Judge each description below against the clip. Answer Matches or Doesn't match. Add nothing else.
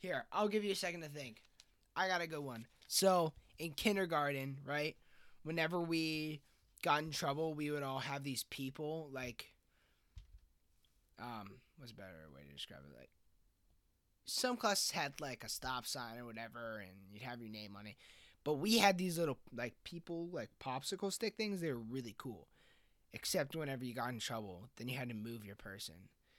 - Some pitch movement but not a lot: Doesn't match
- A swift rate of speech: Doesn't match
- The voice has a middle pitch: Doesn't match